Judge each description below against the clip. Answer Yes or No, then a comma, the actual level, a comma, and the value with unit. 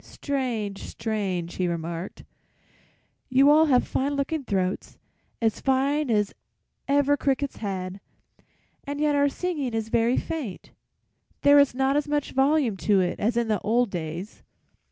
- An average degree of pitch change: No, wide, 6.0 semitones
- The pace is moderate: Yes, average, 145 wpm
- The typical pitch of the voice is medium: No, high, 245 Hz